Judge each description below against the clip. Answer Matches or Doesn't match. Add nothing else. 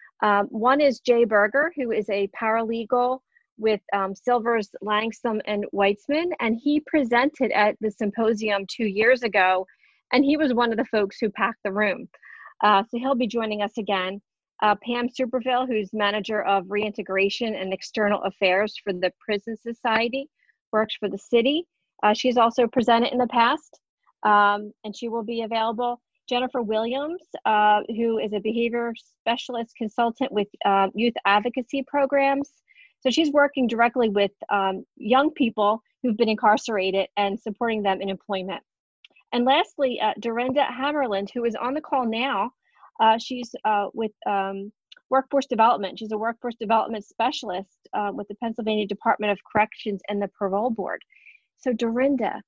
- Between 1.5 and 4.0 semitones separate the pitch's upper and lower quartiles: Matches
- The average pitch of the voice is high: Matches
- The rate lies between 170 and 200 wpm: Doesn't match